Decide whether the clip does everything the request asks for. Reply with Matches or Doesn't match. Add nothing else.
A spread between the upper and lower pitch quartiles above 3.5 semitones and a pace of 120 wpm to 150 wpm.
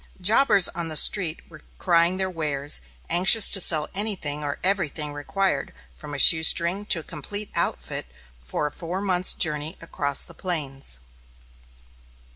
Matches